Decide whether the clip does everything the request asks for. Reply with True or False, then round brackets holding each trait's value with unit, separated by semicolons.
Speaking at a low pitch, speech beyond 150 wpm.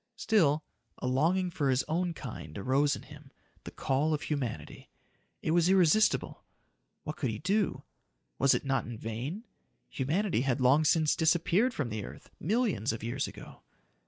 False (150 Hz; 160 wpm)